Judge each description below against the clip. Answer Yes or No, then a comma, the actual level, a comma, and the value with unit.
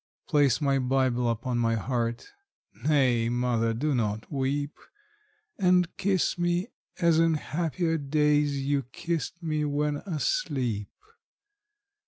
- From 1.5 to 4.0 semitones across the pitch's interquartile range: No, average, 4.7 semitones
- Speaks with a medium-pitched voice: Yes, medium, 145 Hz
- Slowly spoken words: Yes, slow, 115 wpm